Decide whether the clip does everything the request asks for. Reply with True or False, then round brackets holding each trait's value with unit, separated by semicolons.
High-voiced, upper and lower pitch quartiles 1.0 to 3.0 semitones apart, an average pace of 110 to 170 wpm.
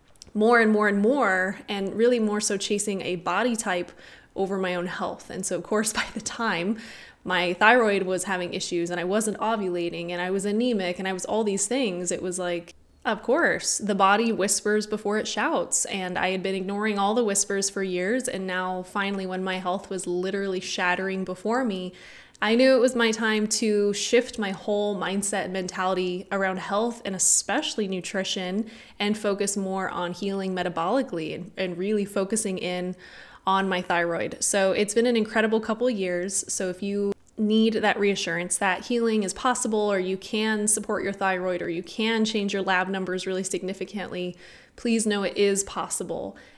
False (195 Hz; 2.6 semitones; 185 wpm)